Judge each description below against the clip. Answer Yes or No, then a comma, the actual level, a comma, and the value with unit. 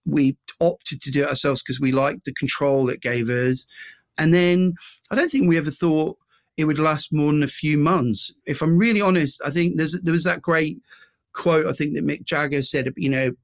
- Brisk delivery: Yes, fast, 225 wpm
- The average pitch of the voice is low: No, medium, 150 Hz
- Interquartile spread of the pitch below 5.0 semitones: Yes, average, 3.4 semitones